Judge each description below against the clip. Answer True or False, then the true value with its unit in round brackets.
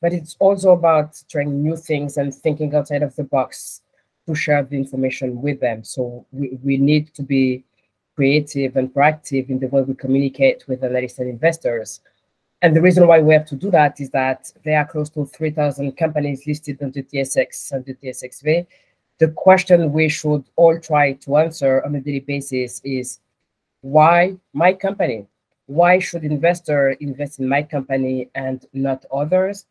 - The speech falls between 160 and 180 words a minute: True (175 wpm)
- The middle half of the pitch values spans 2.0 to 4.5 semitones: True (2.7 semitones)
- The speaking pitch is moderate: True (145 Hz)